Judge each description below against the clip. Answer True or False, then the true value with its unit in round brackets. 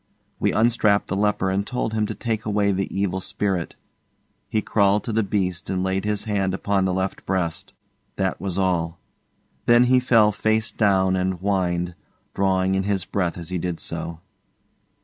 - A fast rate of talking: False (175 wpm)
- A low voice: True (95 Hz)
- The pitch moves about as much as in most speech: False (2.2 semitones)